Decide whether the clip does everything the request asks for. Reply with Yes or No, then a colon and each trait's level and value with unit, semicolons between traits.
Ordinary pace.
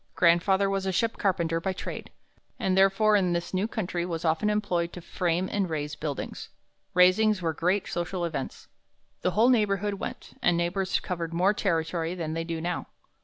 Yes: average, 175 wpm